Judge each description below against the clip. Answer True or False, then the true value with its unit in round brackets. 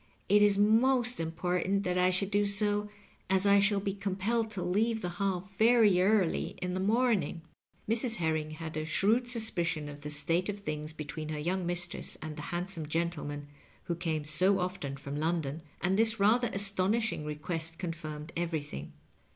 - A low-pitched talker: False (180 Hz)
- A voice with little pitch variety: False (4.3 semitones)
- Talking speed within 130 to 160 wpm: False (175 wpm)